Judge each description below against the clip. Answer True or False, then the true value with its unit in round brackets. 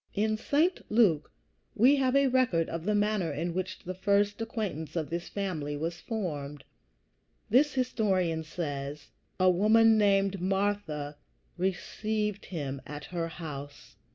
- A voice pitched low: False (185 Hz)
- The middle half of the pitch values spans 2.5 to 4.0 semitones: False (5.0 semitones)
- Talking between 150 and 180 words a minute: False (135 wpm)